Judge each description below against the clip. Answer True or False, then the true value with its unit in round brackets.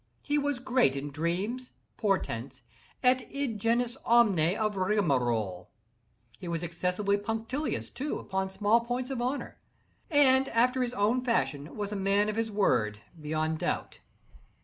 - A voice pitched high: True (210 Hz)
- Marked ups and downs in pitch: True (6.7 semitones)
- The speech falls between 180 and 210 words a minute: False (145 wpm)